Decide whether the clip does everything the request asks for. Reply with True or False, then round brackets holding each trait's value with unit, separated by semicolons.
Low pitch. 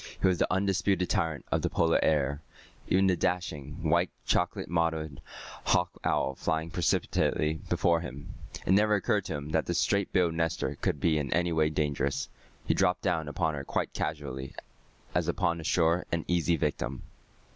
True (80 Hz)